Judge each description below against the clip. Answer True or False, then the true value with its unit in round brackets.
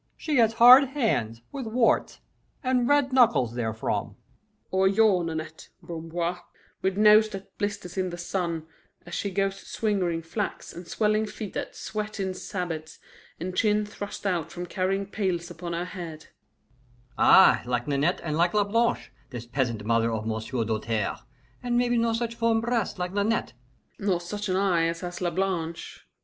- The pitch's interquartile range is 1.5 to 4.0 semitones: False (4.6 semitones)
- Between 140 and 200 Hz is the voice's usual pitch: True (185 Hz)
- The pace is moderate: True (165 wpm)